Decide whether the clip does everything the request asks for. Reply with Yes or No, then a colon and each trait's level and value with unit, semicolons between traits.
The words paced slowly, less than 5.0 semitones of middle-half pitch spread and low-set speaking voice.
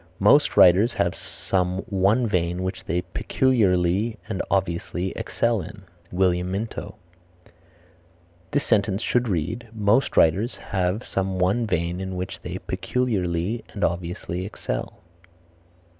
Yes: slow, 120 wpm; average, 3.5 semitones; very low, 95 Hz